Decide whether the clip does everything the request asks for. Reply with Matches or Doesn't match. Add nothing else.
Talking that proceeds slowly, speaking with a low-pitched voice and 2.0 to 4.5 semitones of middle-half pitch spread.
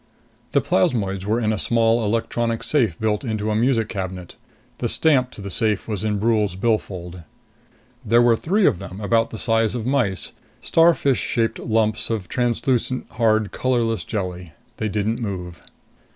Doesn't match